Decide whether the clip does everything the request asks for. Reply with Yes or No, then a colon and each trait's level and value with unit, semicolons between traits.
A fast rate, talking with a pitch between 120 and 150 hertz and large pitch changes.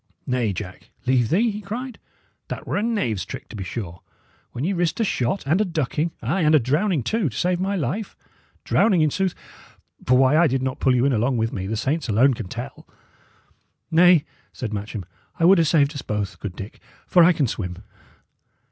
Yes: fast, 210 wpm; medium, 140 Hz; wide, 7.6 semitones